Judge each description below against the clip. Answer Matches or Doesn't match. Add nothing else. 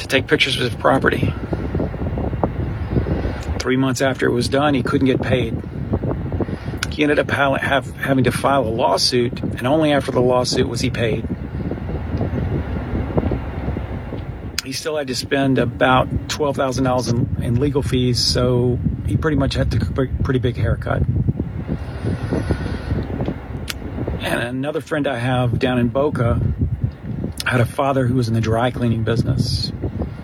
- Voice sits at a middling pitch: Doesn't match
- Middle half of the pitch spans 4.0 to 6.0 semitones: Doesn't match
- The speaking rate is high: Doesn't match